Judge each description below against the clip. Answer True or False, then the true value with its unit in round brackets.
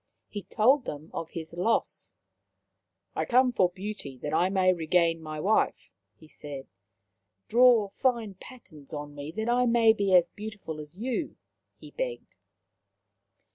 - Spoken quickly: False (155 wpm)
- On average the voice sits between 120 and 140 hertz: False (190 Hz)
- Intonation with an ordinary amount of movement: False (6.7 semitones)